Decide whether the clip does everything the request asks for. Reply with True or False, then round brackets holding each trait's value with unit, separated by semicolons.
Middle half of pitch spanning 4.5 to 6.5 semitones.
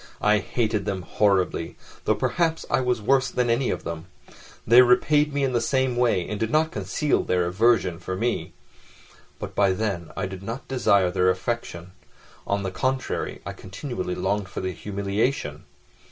True (5.1 semitones)